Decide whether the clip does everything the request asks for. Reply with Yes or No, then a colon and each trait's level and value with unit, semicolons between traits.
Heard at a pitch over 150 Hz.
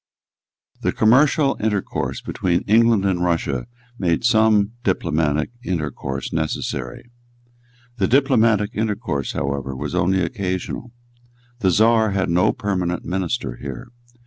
No: very low, 95 Hz